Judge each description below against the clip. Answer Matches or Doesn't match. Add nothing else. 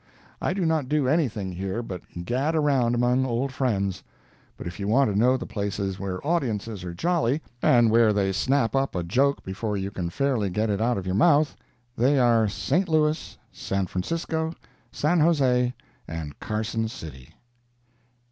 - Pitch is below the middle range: Matches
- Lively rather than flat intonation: Matches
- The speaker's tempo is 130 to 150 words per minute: Doesn't match